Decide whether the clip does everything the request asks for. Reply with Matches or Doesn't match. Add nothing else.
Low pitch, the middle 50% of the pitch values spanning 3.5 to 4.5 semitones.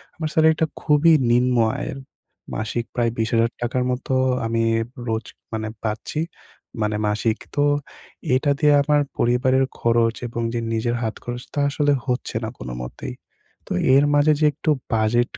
Matches